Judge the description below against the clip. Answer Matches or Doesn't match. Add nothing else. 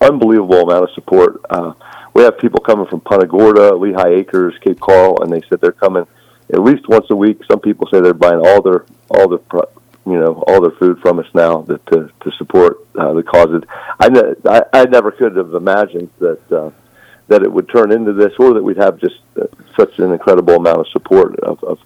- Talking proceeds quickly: Matches